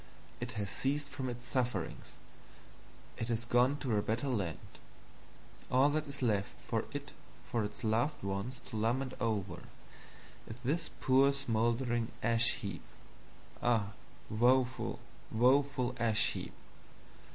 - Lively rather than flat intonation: No, average, 3.0 semitones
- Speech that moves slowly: Yes, slow, 130 wpm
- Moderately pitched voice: No, low, 120 Hz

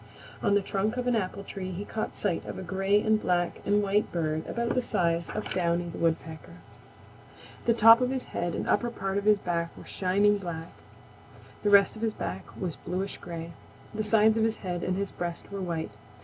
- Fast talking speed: Yes, fast, 210 wpm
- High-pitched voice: Yes, high, 195 Hz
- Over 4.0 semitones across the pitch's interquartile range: No, average, 3.6 semitones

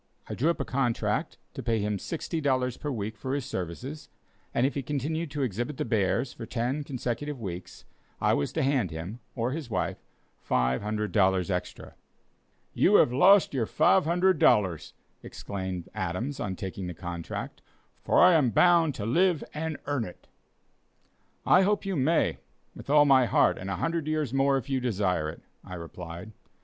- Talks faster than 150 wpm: Yes, average, 170 wpm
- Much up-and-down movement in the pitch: Yes, wide, 7.4 semitones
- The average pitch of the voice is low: Yes, low, 125 Hz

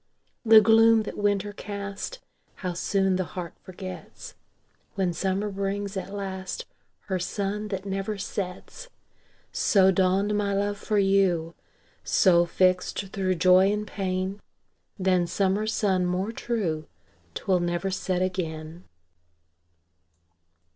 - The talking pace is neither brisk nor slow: No, slow, 120 wpm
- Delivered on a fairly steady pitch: Yes, narrow, 1.8 semitones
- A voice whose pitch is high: Yes, high, 195 Hz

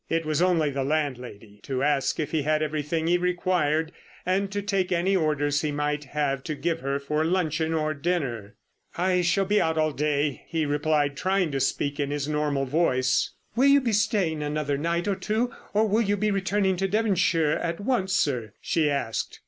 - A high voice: No, medium, 155 Hz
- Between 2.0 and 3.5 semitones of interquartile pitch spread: No, average, 4.2 semitones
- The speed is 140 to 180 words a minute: No, average, 195 wpm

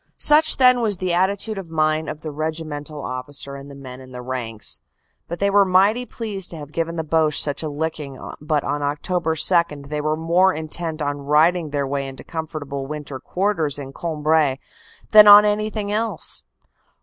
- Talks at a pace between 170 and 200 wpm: Yes, average, 180 wpm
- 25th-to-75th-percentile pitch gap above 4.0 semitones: Yes, average, 4.4 semitones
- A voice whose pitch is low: No, medium, 155 Hz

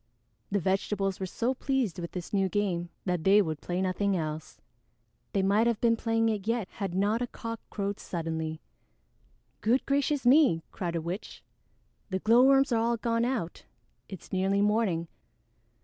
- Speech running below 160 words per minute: No, average, 165 wpm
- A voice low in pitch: No, high, 200 Hz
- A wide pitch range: No, average, 4.3 semitones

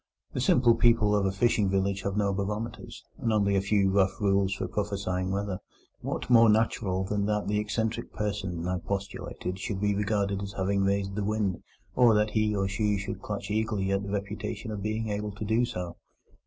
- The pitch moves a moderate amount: No, narrow, 1.6 semitones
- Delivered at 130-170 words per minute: No, average, 195 wpm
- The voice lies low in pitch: Yes, low, 100 Hz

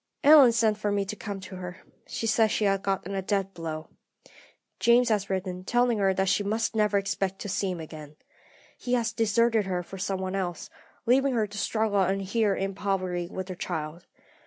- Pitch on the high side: Yes, high, 195 Hz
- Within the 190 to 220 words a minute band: Yes, fast, 205 wpm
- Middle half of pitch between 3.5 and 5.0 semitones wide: No, average, 2.8 semitones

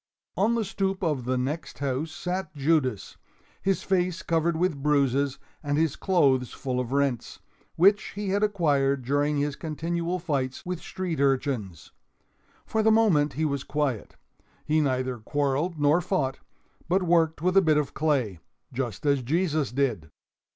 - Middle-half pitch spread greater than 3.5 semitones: Yes, average, 4.6 semitones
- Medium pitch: Yes, medium, 150 Hz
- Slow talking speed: No, average, 155 wpm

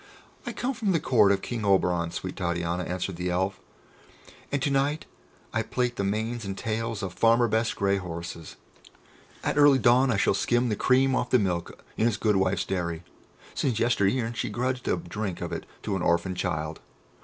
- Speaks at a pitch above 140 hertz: No, low, 105 Hz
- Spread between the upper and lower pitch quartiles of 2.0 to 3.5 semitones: No, average, 5.0 semitones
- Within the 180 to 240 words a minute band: Yes, average, 195 wpm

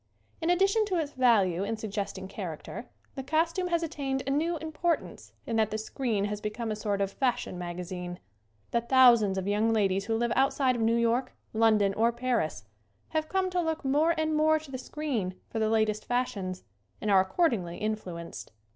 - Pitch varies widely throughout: Yes, wide, 6.6 semitones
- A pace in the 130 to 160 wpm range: No, average, 195 wpm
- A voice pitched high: Yes, high, 230 Hz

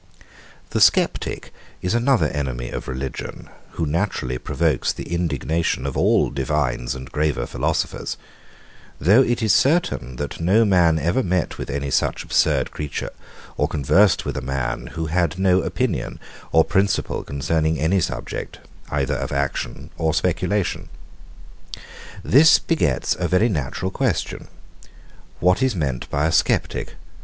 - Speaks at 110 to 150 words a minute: Yes, average, 140 wpm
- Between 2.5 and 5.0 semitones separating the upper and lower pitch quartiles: No, wide, 5.4 semitones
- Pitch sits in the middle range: No, very low, 80 Hz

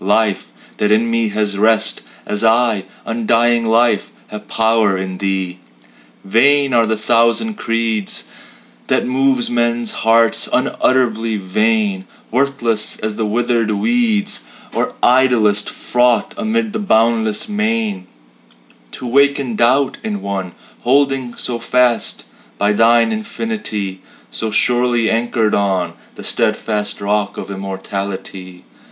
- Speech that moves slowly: Yes, slow, 115 wpm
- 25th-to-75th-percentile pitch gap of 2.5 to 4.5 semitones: Yes, average, 3.3 semitones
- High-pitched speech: No, low, 115 Hz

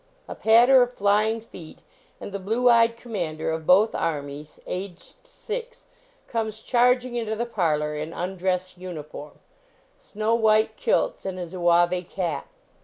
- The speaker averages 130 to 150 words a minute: Yes, average, 140 wpm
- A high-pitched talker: Yes, high, 200 Hz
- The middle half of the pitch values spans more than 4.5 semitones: Yes, average, 4.9 semitones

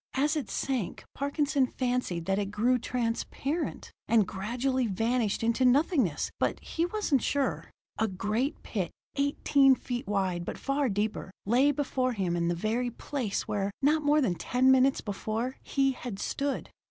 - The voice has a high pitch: Yes, very high, 250 Hz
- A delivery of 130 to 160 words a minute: Yes, average, 155 wpm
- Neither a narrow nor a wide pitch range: Yes, average, 4.9 semitones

